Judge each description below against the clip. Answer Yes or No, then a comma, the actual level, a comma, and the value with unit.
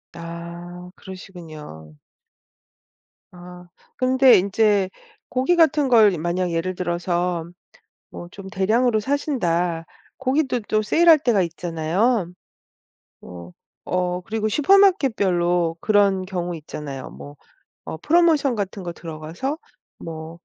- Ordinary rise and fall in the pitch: No, wide, 5.8 semitones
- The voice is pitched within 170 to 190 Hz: Yes, medium, 185 Hz